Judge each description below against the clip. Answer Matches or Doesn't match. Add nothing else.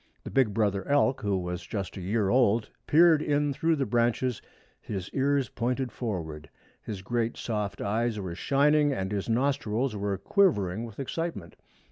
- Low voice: Matches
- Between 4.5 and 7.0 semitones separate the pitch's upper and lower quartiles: Matches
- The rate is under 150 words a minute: Doesn't match